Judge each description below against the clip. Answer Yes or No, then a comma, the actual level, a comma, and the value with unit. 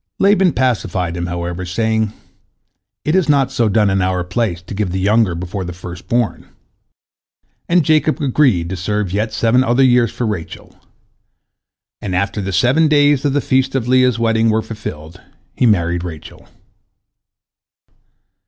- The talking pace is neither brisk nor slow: Yes, average, 160 wpm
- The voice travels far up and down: Yes, wide, 5.9 semitones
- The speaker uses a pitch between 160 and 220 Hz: No, low, 110 Hz